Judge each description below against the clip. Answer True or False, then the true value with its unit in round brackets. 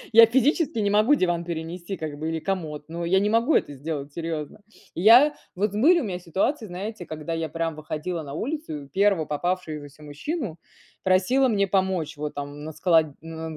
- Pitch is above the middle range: False (175 Hz)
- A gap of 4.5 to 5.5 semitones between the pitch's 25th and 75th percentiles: True (4.9 semitones)